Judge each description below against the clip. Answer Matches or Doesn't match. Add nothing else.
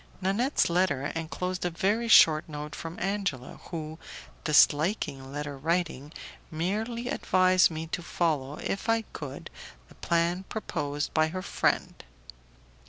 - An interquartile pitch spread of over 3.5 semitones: Matches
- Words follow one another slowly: Matches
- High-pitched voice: Doesn't match